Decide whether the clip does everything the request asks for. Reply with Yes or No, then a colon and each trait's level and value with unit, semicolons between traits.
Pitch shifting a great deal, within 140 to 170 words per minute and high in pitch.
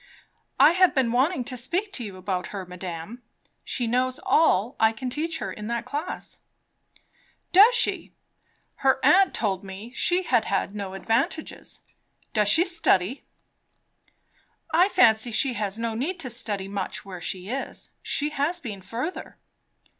Yes: wide, 6.9 semitones; average, 155 wpm; high, 240 Hz